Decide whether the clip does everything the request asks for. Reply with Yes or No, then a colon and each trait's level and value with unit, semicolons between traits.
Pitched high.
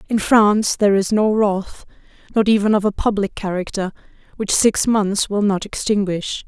Yes: high, 205 Hz